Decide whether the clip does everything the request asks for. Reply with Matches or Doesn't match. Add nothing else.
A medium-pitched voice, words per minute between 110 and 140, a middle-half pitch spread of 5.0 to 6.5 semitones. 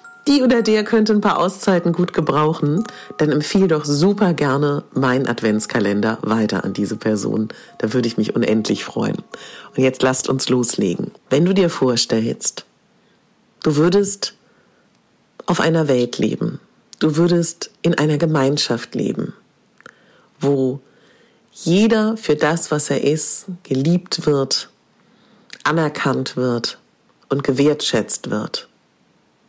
Matches